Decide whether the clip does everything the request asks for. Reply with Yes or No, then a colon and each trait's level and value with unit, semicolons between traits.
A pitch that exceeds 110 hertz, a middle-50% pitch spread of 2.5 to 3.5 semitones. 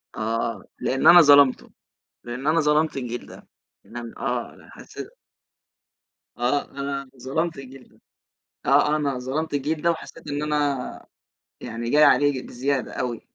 Yes: medium, 140 Hz; average, 3.1 semitones